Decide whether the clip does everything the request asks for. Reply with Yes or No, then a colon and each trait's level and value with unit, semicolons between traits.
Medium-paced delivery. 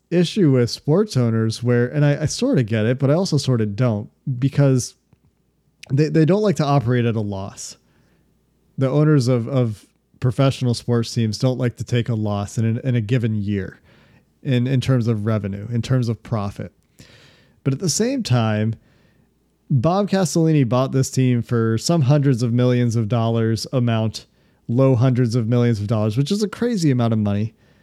Yes: average, 190 wpm